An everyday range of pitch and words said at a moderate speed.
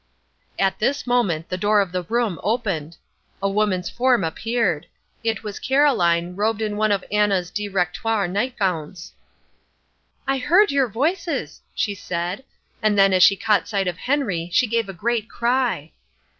Yes: average, 4.7 semitones; average, 155 wpm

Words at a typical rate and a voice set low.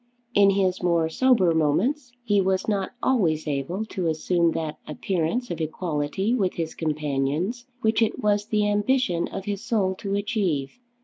No: average, 160 wpm; high, 190 Hz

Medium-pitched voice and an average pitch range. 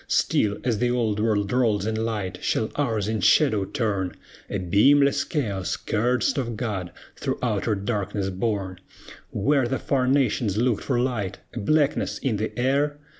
No: low, 110 Hz; average, 4.0 semitones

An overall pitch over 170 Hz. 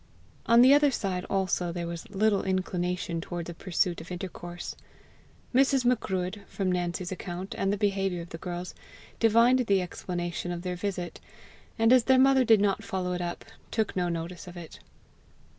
Yes: medium, 185 Hz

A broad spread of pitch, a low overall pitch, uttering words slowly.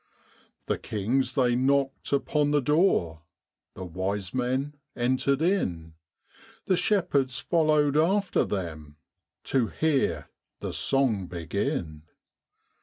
Yes: wide, 7.6 semitones; low, 130 Hz; slow, 105 wpm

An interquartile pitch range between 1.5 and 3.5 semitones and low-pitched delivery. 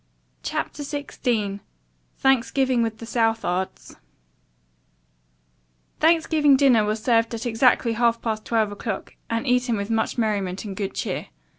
No: average, 2.8 semitones; high, 230 Hz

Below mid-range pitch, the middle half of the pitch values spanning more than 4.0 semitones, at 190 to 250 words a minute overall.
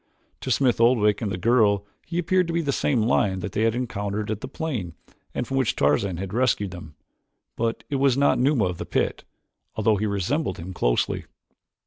Yes: low, 110 Hz; average, 4.9 semitones; average, 200 wpm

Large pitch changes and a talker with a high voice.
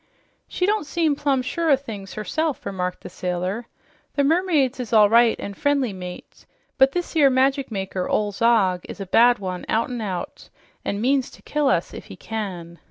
Yes: wide, 6.2 semitones; high, 235 Hz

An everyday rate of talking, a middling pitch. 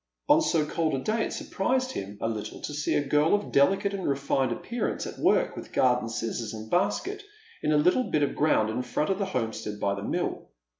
No: fast, 220 wpm; medium, 150 Hz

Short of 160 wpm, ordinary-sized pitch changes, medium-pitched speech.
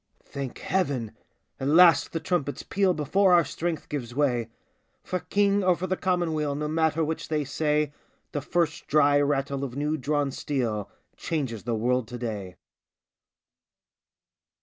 Yes: average, 150 wpm; average, 3.9 semitones; medium, 150 Hz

